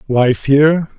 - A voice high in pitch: No, medium, 140 Hz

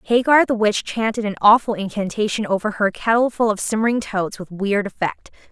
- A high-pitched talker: Yes, high, 215 Hz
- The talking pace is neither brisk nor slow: Yes, average, 175 wpm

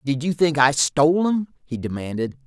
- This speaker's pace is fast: No, average, 195 wpm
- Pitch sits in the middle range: Yes, medium, 145 Hz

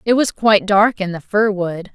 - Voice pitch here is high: Yes, high, 200 Hz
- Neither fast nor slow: No, fast, 245 wpm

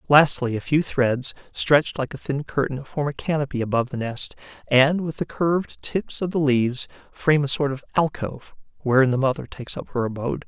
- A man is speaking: Yes, male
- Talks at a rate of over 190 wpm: Yes, average, 200 wpm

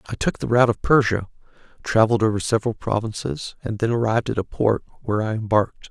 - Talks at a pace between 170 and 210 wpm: Yes, average, 195 wpm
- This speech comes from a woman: No, male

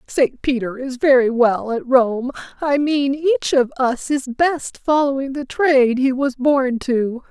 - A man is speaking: No, female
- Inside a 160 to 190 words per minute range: Yes, average, 170 wpm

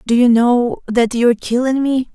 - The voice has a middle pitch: No, high, 240 Hz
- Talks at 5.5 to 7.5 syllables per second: No, 5.2 syllables/s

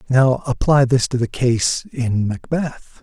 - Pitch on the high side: No, low, 125 Hz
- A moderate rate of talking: Yes, average, 160 wpm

